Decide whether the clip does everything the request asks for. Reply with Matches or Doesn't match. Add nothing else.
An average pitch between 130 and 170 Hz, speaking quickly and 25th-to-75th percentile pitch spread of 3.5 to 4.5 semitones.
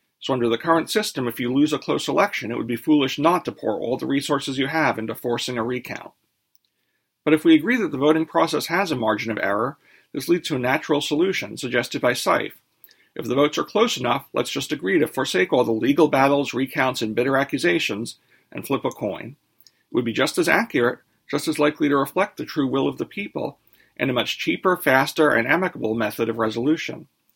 Matches